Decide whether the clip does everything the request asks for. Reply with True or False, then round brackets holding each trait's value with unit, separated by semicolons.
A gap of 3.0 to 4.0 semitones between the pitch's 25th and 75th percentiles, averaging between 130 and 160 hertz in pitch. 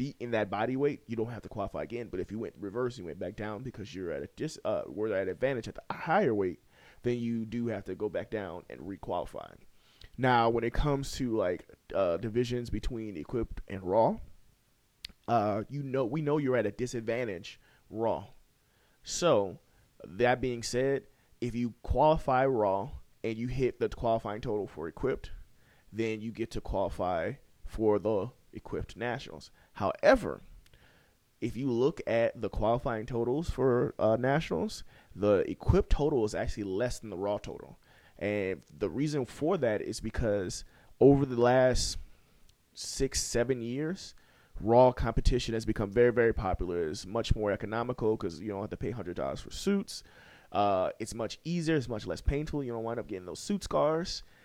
False (3.3 semitones; 115 Hz)